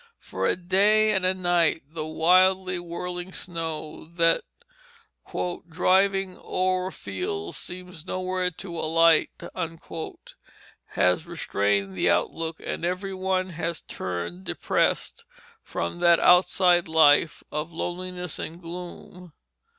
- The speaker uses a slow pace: Yes, slow, 110 wpm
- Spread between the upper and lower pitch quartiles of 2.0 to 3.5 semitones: Yes, narrow, 2.5 semitones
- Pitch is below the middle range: No, medium, 175 Hz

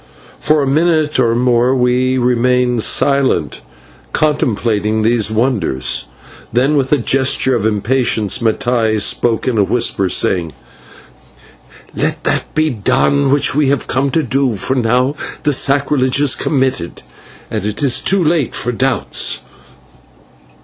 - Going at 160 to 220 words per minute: No, slow, 135 wpm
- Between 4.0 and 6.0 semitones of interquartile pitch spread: No, average, 3.5 semitones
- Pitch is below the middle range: Yes, low, 125 Hz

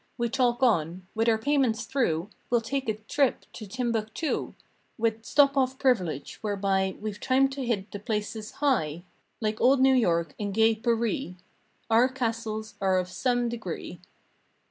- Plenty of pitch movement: No, average, 3.9 semitones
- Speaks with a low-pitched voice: No, high, 225 Hz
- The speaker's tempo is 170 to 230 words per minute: No, average, 155 wpm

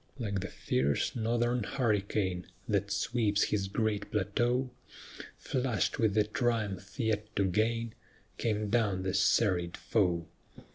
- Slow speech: Yes, slow, 125 wpm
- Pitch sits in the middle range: No, low, 105 Hz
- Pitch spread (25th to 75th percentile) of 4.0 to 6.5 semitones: No, average, 2.8 semitones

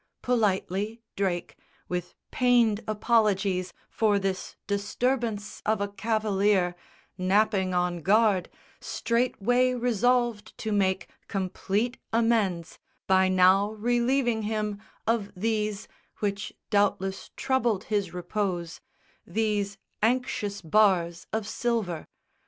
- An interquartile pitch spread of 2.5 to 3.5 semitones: Yes, average, 3.0 semitones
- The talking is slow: Yes, slow, 95 wpm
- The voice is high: Yes, high, 210 Hz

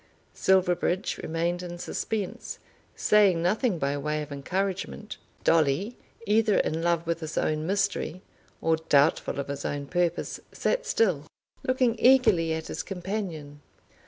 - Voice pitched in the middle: Yes, medium, 175 Hz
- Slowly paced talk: Yes, slow, 130 wpm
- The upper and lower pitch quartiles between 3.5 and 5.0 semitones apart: Yes, average, 4.4 semitones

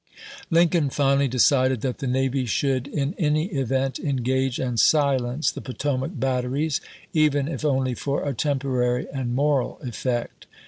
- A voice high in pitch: No, low, 135 Hz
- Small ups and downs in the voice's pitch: Yes, narrow, 2.0 semitones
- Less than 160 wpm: Yes, average, 140 wpm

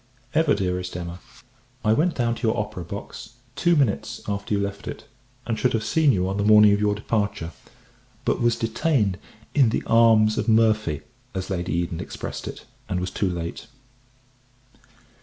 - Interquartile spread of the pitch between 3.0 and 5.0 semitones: Yes, average, 3.6 semitones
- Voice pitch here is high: No, low, 105 Hz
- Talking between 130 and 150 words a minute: No, average, 175 wpm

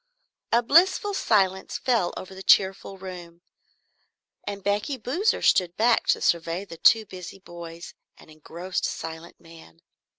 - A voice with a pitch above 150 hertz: Yes, high, 190 Hz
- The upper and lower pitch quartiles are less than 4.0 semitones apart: No, average, 4.5 semitones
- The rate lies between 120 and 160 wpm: Yes, slow, 135 wpm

